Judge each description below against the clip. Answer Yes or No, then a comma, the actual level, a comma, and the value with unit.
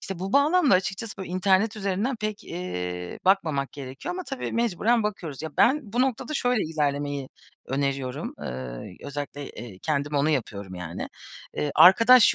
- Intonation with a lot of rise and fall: Yes, wide, 8.1 semitones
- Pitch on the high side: No, medium, 160 Hz